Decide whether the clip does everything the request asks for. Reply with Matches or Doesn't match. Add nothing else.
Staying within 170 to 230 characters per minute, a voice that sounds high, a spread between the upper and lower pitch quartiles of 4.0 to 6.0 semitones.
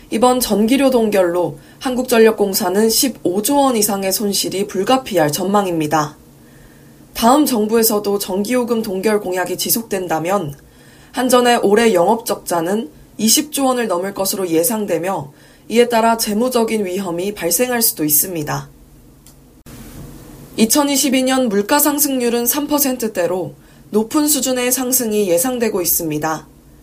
Doesn't match